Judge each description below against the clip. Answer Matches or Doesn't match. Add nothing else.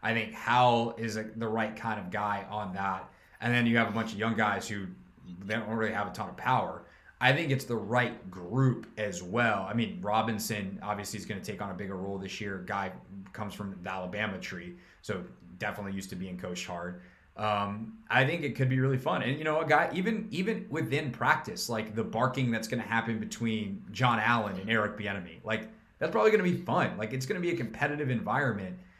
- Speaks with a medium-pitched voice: Doesn't match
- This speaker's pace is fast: Matches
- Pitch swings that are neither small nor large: Matches